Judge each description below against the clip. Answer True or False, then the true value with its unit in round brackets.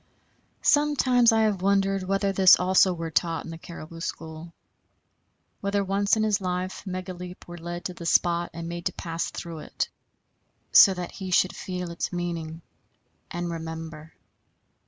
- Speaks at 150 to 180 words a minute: True (155 wpm)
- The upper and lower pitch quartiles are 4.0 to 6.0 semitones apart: False (2.7 semitones)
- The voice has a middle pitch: True (180 Hz)